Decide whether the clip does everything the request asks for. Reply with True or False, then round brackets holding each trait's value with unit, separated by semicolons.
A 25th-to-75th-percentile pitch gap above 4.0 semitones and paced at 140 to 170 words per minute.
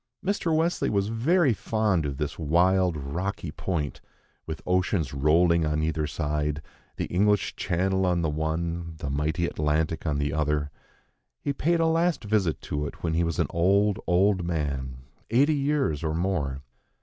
True (4.9 semitones; 160 wpm)